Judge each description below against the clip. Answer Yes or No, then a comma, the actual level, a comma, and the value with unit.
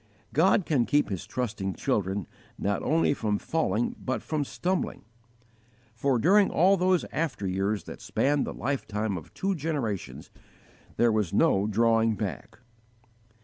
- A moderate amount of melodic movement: No, wide, 7.2 semitones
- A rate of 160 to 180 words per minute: No, average, 140 wpm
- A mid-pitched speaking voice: No, low, 120 Hz